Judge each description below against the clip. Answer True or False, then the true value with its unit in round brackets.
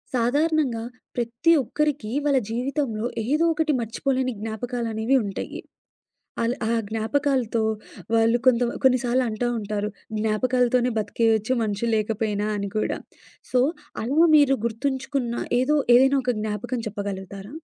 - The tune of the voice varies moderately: True (3.4 semitones)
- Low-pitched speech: False (235 Hz)